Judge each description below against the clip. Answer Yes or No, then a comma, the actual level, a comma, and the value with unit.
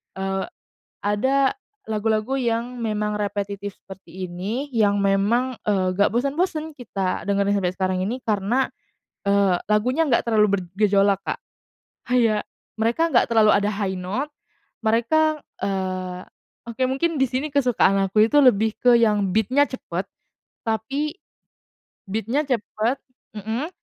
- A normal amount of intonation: Yes, average, 4.2 semitones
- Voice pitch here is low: No, high, 215 Hz